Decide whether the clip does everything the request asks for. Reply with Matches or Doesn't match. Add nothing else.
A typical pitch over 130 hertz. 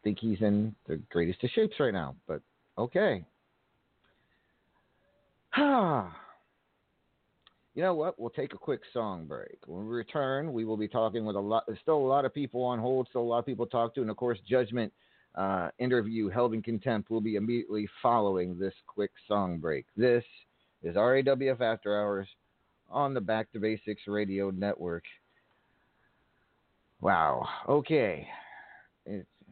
Doesn't match